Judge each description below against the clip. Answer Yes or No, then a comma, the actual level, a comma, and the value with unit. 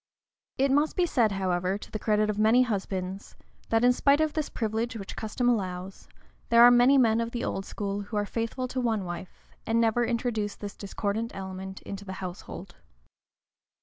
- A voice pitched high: Yes, high, 220 Hz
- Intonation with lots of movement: No, average, 3.6 semitones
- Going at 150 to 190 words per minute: Yes, average, 185 wpm